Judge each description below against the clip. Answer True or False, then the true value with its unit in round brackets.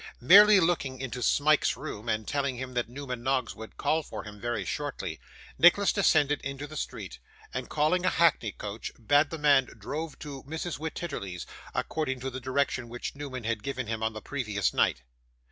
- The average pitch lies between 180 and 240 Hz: False (135 Hz)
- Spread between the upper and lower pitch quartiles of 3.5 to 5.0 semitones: True (4.3 semitones)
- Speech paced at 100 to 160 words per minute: False (180 wpm)